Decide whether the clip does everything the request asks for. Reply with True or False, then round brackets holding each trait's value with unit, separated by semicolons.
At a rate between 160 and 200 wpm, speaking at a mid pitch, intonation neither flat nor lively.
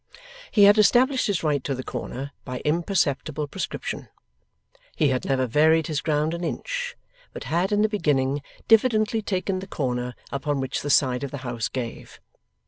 False (170 wpm; 150 Hz; 7.1 semitones)